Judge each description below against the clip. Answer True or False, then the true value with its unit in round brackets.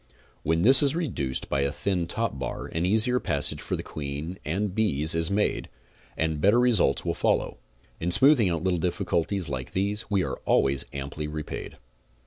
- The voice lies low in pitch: True (90 Hz)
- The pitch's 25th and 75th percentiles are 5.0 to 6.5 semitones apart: True (5.6 semitones)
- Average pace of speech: True (175 wpm)